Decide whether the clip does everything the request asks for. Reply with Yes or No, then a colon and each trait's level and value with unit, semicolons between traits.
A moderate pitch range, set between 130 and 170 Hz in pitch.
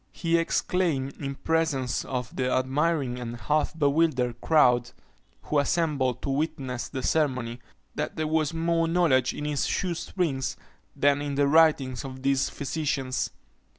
Yes: average, 3.7 semitones; medium, 140 Hz